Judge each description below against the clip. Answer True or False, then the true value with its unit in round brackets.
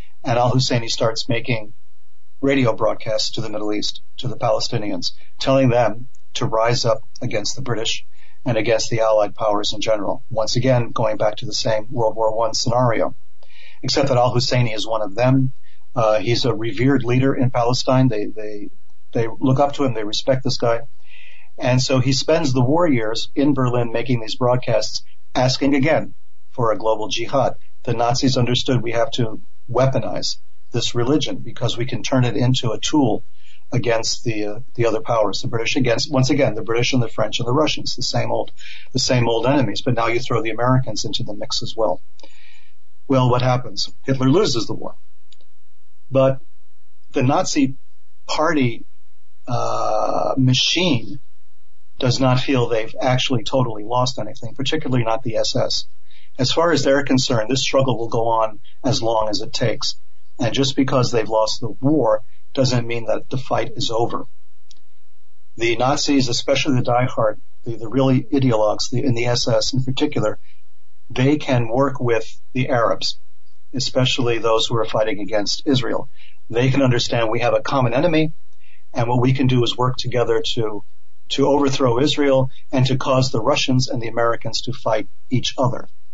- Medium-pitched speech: False (125 Hz)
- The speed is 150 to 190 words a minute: True (175 wpm)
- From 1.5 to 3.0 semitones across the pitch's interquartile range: True (2.6 semitones)